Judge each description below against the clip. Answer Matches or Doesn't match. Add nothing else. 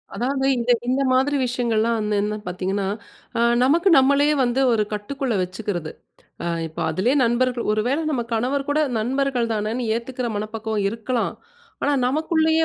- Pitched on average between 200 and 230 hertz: Doesn't match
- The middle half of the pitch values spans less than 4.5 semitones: Matches